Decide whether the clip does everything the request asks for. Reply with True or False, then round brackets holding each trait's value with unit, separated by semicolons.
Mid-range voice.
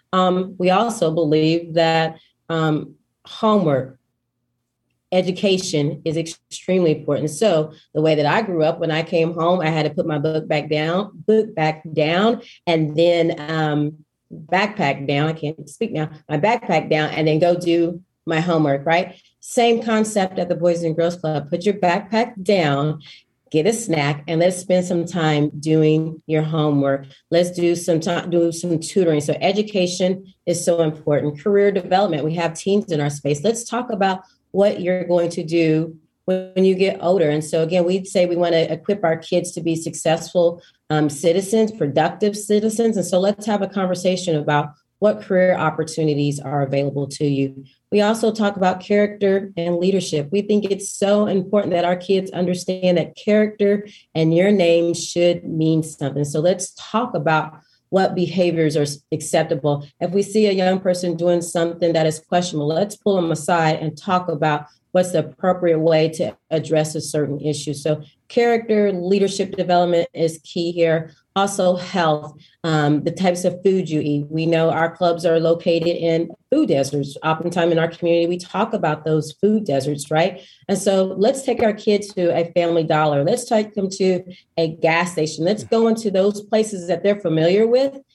True (170 Hz)